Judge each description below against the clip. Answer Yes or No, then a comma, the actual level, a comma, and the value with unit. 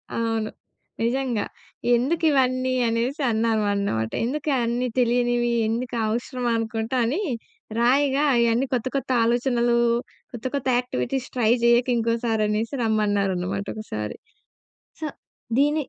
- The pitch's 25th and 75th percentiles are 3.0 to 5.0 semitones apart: No, narrow, 2.5 semitones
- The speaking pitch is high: Yes, high, 235 Hz